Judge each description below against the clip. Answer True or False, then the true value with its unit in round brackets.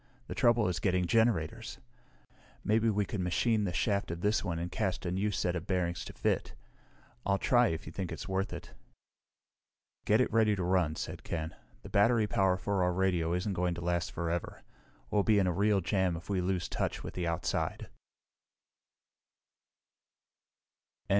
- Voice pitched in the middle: False (95 Hz)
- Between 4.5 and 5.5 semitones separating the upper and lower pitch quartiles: False (3.0 semitones)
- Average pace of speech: True (175 wpm)